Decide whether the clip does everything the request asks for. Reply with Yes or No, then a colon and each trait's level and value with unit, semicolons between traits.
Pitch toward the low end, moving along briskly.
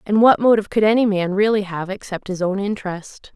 No: high, 200 Hz; fast, 215 wpm